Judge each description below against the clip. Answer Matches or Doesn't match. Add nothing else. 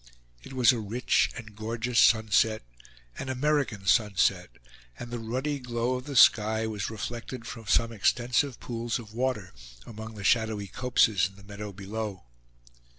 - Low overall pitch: Matches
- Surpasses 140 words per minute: Matches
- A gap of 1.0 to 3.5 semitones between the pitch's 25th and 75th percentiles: Matches